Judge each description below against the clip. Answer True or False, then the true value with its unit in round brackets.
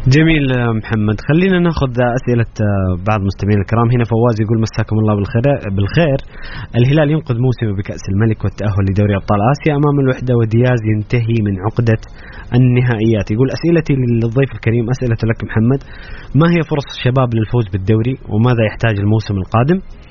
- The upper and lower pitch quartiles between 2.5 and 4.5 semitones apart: True (3.2 semitones)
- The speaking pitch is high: False (115 Hz)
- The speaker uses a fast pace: True (145 wpm)